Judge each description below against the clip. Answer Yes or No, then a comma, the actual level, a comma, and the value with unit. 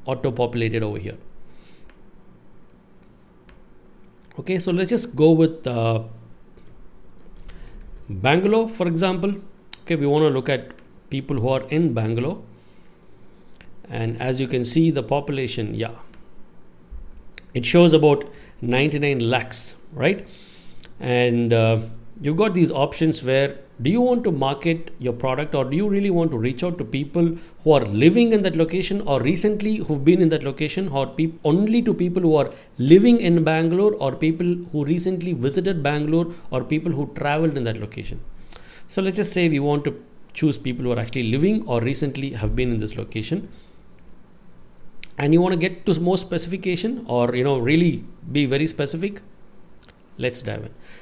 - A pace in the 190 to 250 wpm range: No, average, 160 wpm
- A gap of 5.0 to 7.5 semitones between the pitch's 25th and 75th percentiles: Yes, wide, 5.6 semitones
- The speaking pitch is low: No, medium, 150 Hz